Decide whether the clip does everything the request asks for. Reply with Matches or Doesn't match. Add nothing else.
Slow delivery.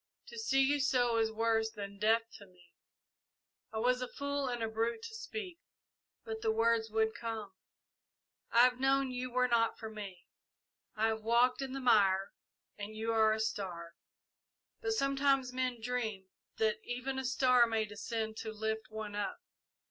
Doesn't match